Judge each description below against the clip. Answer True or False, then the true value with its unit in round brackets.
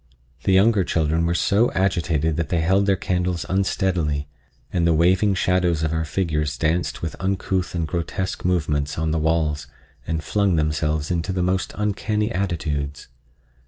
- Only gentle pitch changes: False (3.2 semitones)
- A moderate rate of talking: True (160 wpm)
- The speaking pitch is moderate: False (85 Hz)